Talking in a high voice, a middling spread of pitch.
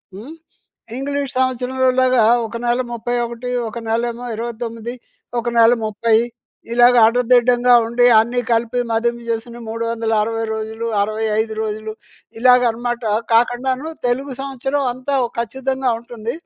No: high, 235 Hz; narrow, 1.7 semitones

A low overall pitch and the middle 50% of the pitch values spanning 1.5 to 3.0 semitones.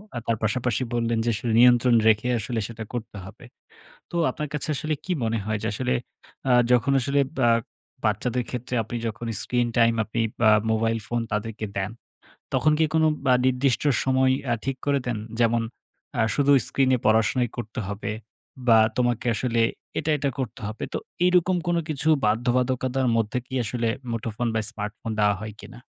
Yes: low, 120 Hz; narrow, 2.6 semitones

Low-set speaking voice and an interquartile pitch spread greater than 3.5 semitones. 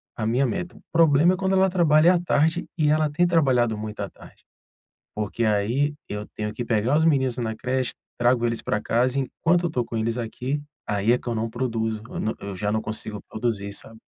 Yes: low, 120 Hz; wide, 5.6 semitones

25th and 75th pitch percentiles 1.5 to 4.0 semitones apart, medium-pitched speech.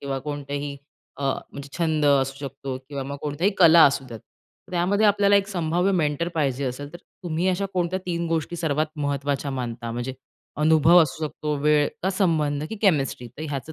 Yes: average, 3.6 semitones; medium, 150 Hz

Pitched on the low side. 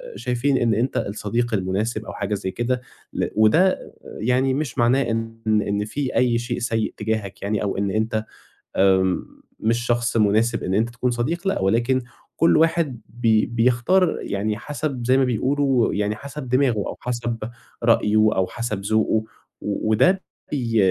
Yes: low, 115 Hz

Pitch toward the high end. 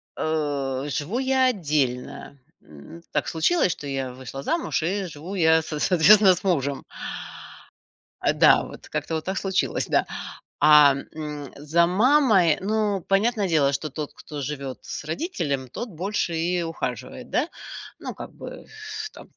No: medium, 160 Hz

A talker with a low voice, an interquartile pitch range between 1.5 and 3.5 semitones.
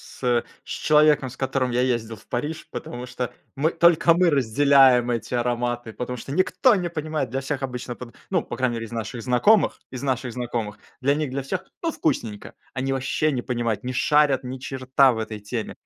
Yes: low, 130 Hz; average, 3.2 semitones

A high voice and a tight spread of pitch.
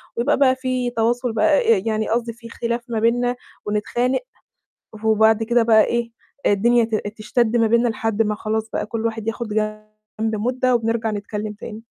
Yes: high, 225 Hz; narrow, 1.8 semitones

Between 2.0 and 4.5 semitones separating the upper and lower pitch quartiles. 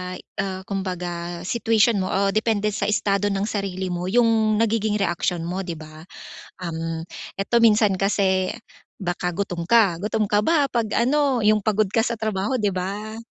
Yes: average, 3.0 semitones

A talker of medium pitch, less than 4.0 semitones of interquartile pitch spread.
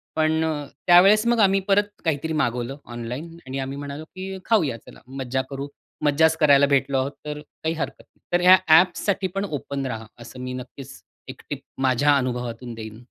No: medium, 145 Hz; average, 4.3 semitones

